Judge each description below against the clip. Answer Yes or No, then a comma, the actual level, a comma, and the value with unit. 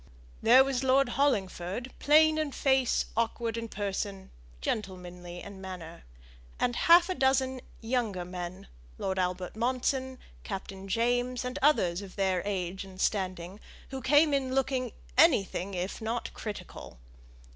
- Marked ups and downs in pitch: Yes, wide, 5.7 semitones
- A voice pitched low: No, high, 225 Hz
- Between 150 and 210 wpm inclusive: No, slow, 135 wpm